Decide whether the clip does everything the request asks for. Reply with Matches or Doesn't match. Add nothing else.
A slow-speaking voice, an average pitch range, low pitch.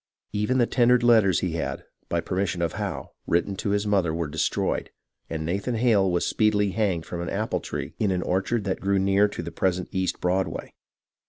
Doesn't match